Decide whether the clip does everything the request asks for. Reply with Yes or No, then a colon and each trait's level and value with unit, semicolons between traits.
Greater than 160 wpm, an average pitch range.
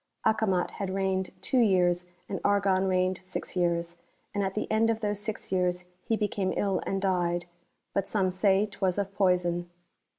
No: average, 170 wpm; narrow, 2.1 semitones